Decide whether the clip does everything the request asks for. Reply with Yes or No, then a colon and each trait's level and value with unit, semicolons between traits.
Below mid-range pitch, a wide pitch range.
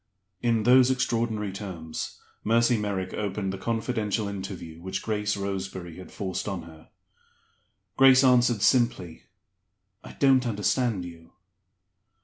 No: low, 105 Hz; average, 3.9 semitones